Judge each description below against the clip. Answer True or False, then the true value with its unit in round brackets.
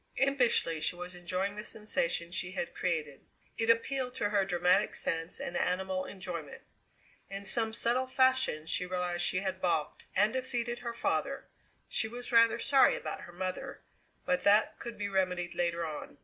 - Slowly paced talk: False (165 wpm)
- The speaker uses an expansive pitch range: False (4.8 semitones)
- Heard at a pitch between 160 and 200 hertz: True (190 Hz)